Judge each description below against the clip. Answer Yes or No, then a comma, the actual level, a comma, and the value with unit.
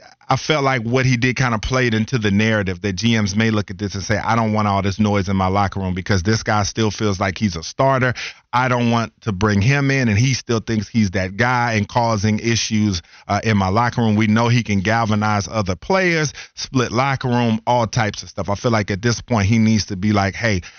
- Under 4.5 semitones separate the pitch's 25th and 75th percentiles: Yes, average, 2.9 semitones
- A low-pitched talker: Yes, low, 110 Hz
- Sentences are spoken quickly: Yes, fast, 250 wpm